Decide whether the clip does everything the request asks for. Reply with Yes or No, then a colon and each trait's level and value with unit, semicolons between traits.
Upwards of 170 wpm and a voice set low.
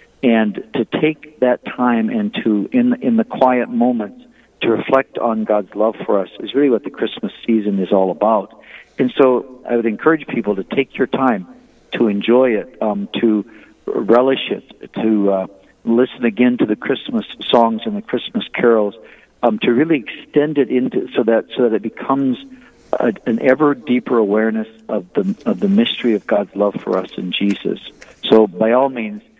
Yes: average, 185 wpm; low, 125 Hz